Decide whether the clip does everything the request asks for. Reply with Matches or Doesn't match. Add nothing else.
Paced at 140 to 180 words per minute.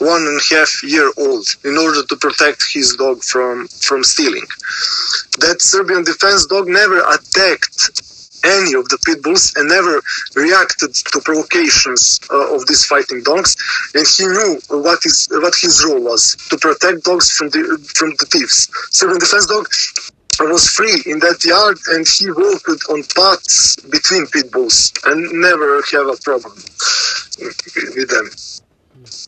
Matches